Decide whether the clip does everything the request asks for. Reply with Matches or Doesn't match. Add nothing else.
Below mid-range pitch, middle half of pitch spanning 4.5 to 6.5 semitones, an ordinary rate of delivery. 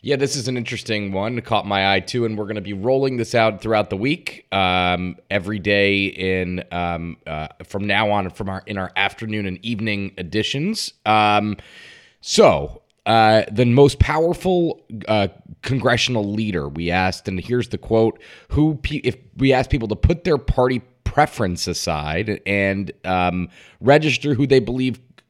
Matches